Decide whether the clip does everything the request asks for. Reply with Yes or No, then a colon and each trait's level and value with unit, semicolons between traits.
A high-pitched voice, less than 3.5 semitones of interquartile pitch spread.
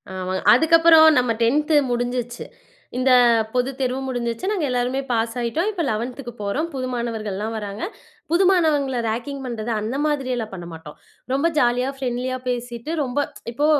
Yes: very high, 250 Hz; average, 3.0 semitones